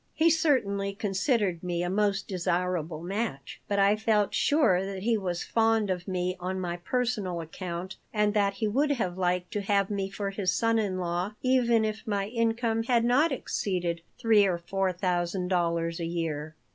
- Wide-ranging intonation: No, average, 3.7 semitones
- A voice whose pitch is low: No, high, 195 Hz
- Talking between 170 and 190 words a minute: Yes, average, 180 wpm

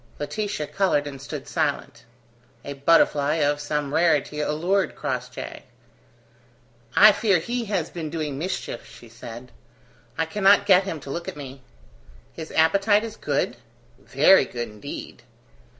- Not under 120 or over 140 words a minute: Yes, slow, 135 wpm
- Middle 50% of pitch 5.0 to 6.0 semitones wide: Yes, average, 5.3 semitones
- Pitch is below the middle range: No, medium, 155 Hz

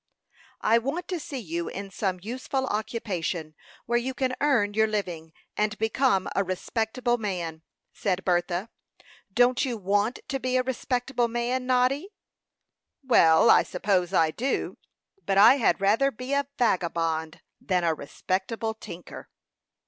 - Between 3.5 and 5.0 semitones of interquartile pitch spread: No, wide, 5.6 semitones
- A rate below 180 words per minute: Yes, average, 140 wpm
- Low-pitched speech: No, high, 220 Hz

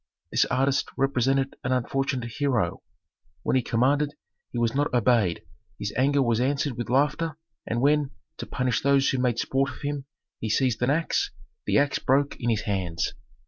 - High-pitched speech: No, low, 130 Hz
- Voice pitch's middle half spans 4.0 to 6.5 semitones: No, average, 2.9 semitones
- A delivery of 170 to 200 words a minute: Yes, average, 175 wpm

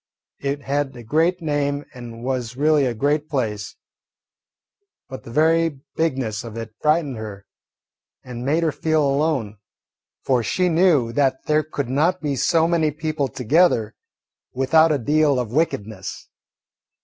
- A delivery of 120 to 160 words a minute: Yes, average, 145 wpm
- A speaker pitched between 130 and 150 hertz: Yes, medium, 140 Hz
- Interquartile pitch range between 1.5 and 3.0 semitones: No, average, 4.5 semitones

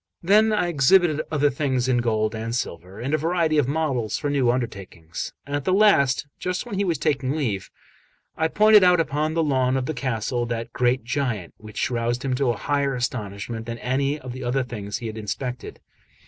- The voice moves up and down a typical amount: Yes, average, 4.5 semitones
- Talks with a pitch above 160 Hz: No, low, 130 Hz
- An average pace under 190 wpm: No, average, 195 wpm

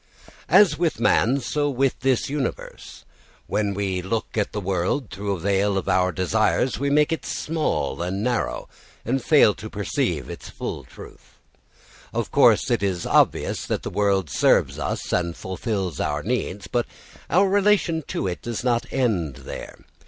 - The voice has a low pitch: Yes, low, 105 Hz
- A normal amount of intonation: No, wide, 6.2 semitones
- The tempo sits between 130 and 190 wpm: Yes, average, 165 wpm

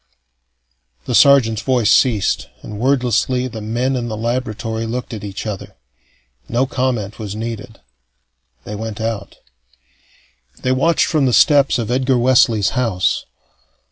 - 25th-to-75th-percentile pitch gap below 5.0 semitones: Yes, average, 3.0 semitones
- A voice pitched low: Yes, low, 115 Hz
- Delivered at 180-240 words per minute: No, slow, 135 wpm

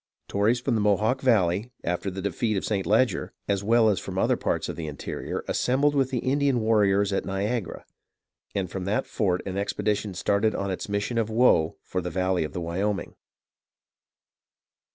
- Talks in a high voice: No, low, 100 Hz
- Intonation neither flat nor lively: Yes, average, 3.3 semitones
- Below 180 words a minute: No, average, 185 wpm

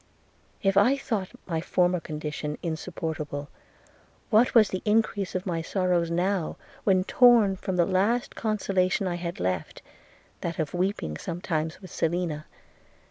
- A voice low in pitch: No, medium, 180 Hz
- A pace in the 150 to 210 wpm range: No, average, 140 wpm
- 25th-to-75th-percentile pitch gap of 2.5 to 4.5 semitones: Yes, average, 3.3 semitones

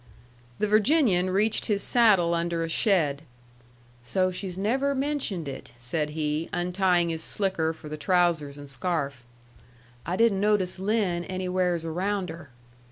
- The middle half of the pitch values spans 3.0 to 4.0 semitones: Yes, average, 3.7 semitones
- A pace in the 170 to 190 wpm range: No, average, 140 wpm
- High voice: No, medium, 180 Hz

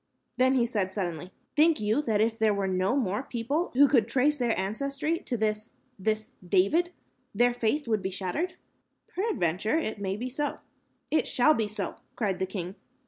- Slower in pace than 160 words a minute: No, average, 180 wpm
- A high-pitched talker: Yes, high, 225 Hz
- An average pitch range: No, wide, 5.8 semitones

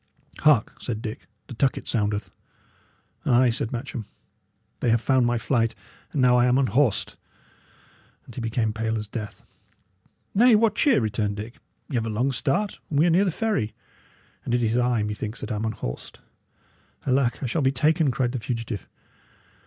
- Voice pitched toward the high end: No, low, 120 Hz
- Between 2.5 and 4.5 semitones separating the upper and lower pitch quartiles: Yes, average, 3.4 semitones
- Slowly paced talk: No, average, 175 wpm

